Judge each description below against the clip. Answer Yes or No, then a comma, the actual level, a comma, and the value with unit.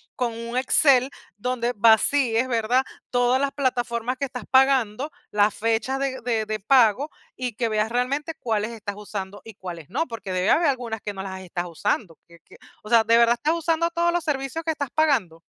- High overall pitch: Yes, high, 240 Hz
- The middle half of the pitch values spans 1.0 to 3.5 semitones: No, average, 4.0 semitones